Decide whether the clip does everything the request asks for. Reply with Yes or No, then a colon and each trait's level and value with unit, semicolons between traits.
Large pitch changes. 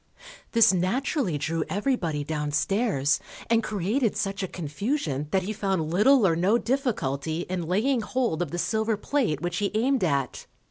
Yes: wide, 6.1 semitones